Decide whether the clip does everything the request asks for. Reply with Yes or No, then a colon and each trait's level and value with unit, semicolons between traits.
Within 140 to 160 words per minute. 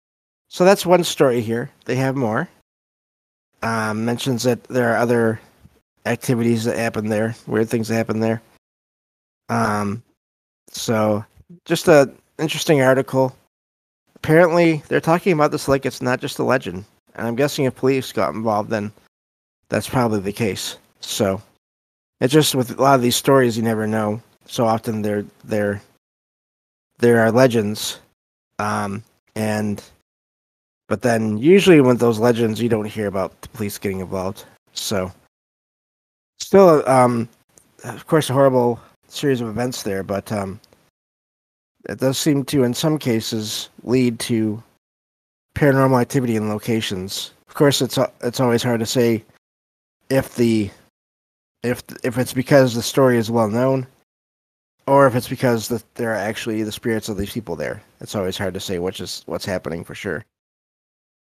Yes: average, 155 wpm